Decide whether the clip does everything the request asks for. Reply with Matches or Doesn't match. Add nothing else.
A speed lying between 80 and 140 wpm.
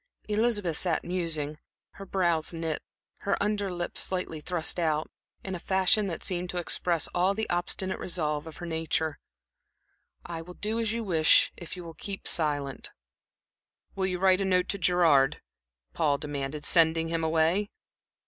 Doesn't match